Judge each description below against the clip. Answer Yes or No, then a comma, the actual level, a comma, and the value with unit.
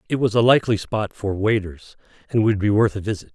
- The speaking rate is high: Yes, fast, 235 wpm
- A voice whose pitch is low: Yes, low, 105 Hz